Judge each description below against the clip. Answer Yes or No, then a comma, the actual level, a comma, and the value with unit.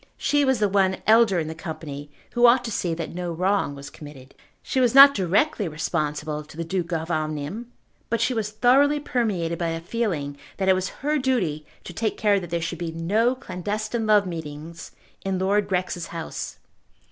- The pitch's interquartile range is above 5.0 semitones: Yes, wide, 5.4 semitones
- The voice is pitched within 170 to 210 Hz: Yes, medium, 185 Hz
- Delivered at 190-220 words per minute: Yes, average, 195 wpm